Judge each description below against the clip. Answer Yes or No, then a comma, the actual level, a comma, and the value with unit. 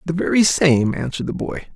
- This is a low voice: No, medium, 145 Hz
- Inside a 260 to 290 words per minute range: No, fast, 205 wpm